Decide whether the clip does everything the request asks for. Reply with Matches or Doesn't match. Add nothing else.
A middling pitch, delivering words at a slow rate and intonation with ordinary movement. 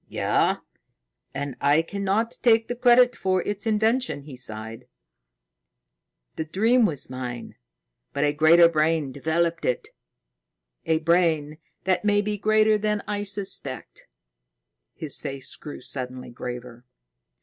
Doesn't match